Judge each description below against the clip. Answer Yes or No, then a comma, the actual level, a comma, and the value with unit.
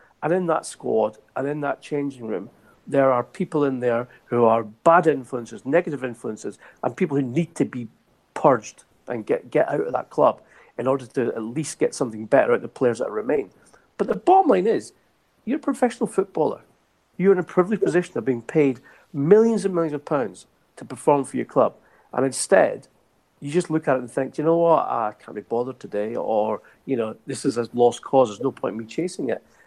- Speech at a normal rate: No, fast, 215 wpm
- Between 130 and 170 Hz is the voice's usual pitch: Yes, medium, 140 Hz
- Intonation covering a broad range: Yes, wide, 5.7 semitones